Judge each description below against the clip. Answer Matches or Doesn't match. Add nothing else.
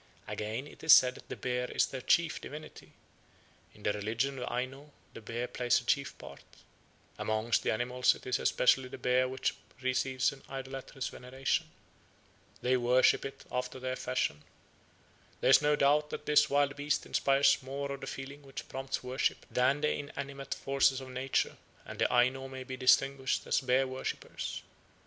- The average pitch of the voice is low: Matches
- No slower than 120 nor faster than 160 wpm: Doesn't match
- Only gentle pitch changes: Matches